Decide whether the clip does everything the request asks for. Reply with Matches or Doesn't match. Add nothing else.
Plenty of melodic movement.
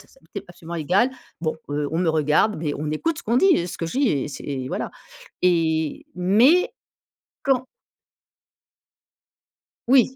Matches